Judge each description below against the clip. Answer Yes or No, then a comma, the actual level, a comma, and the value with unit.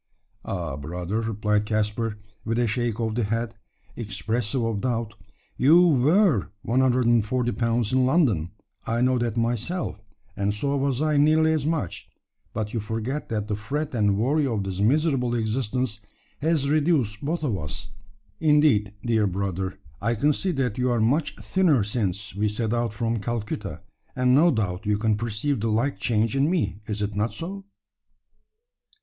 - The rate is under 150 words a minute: No, average, 165 wpm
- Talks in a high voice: No, low, 115 Hz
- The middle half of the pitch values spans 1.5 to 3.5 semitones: No, average, 4.5 semitones